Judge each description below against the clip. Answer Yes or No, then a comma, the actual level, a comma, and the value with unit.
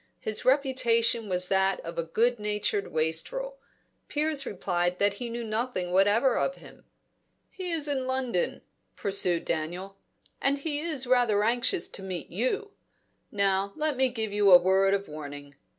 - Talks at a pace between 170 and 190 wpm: No, average, 155 wpm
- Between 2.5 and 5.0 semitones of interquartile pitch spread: No, wide, 5.6 semitones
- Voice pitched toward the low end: No, high, 215 Hz